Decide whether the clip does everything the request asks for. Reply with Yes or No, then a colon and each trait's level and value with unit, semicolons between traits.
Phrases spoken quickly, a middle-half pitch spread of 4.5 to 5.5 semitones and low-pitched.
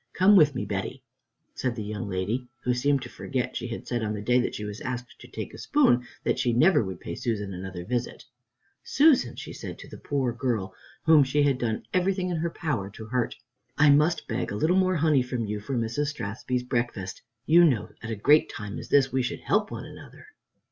Yes: fast, 225 wpm; average, 5.2 semitones; low, 125 Hz